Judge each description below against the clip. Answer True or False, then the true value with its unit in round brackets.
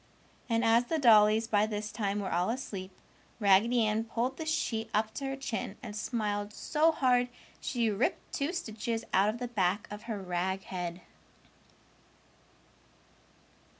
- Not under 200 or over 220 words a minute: False (150 wpm)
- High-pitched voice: True (220 Hz)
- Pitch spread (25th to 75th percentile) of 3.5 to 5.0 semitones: False (3.0 semitones)